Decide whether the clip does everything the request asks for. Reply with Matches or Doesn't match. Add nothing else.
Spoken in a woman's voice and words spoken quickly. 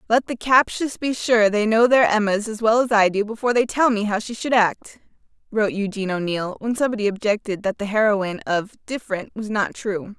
Matches